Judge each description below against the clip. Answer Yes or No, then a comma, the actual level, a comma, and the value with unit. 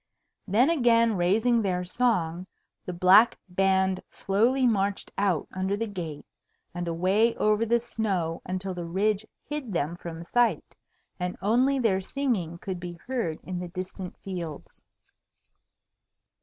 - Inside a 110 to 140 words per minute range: Yes, slow, 135 wpm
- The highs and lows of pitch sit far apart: No, average, 4.3 semitones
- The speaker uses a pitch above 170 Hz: Yes, high, 190 Hz